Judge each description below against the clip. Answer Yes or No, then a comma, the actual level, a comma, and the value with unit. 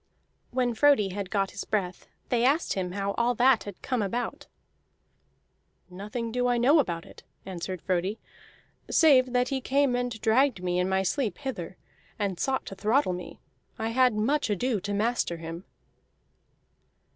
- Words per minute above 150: Yes, average, 160 wpm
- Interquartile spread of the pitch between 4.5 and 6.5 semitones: Yes, average, 4.9 semitones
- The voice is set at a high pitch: Yes, high, 220 Hz